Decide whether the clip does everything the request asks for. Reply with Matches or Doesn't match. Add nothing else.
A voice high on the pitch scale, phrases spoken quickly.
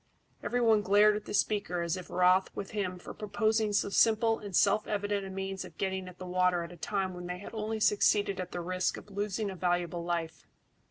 Matches